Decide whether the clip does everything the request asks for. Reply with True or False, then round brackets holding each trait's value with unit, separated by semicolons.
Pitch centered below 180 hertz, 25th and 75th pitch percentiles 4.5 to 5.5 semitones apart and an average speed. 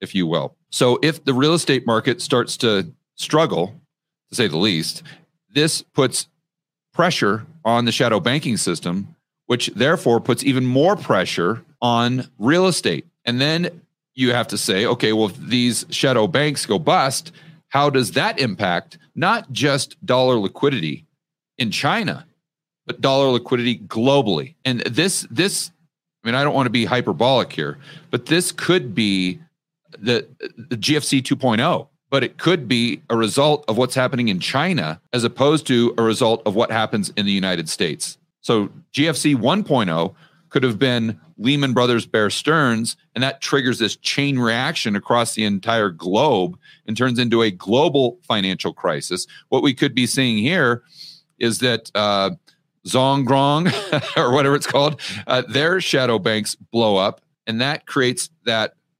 True (135 Hz; 5.0 semitones; 160 wpm)